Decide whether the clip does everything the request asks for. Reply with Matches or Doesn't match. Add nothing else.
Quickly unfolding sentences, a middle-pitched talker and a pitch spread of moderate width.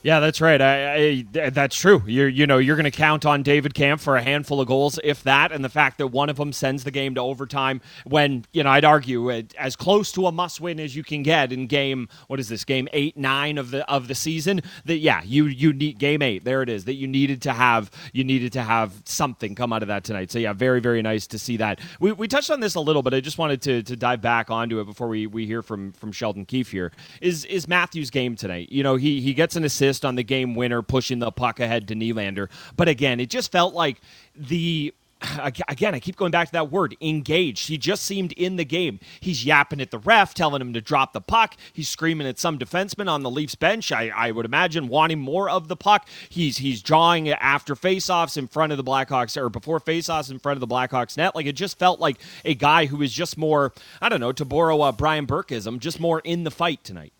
Matches